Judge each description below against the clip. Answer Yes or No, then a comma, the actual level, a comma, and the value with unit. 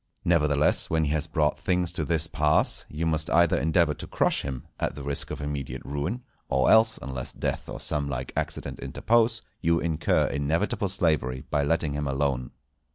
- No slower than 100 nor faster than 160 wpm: No, average, 180 wpm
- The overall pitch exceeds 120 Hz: No, very low, 75 Hz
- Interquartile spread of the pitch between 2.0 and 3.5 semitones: Yes, average, 2.8 semitones